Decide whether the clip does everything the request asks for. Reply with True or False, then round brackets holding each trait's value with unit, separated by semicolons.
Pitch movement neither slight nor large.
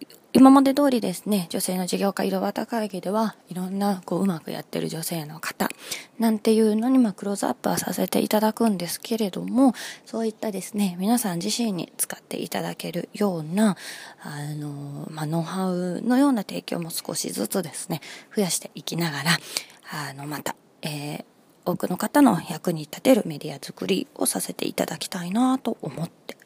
True (4.6 semitones)